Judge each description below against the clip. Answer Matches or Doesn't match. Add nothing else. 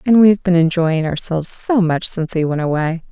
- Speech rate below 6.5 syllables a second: Matches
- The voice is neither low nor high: Matches